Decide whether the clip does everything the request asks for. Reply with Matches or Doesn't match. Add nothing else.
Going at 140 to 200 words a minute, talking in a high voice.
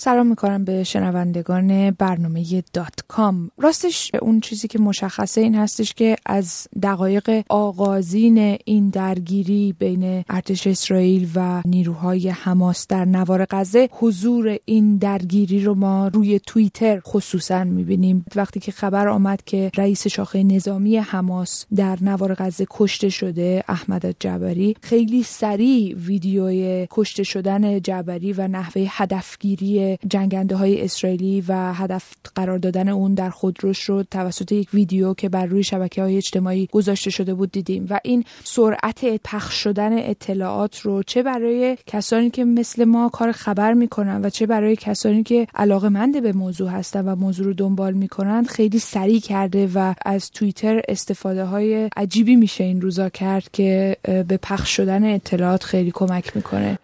Matches